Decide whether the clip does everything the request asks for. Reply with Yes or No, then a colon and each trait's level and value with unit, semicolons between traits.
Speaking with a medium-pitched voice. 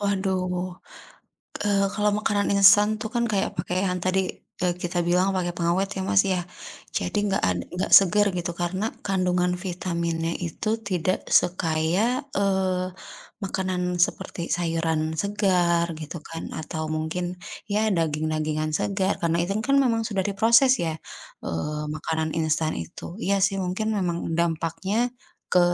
Yes: medium, 180 Hz